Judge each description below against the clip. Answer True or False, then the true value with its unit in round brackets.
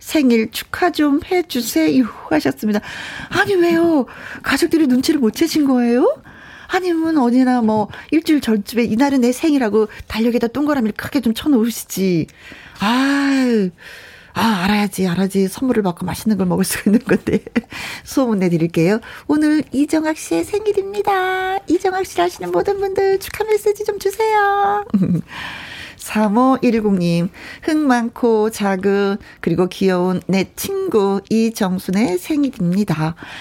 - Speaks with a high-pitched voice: True (245 Hz)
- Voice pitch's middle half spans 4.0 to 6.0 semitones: False (7.8 semitones)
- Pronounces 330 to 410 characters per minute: False (295 characters per minute)